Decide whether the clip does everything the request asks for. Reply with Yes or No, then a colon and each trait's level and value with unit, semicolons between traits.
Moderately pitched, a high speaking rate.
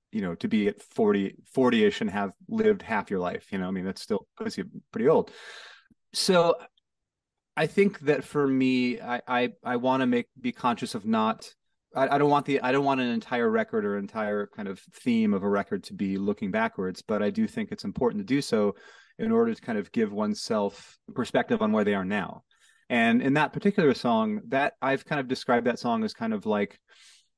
Yes: medium, 175 Hz; fast, 220 wpm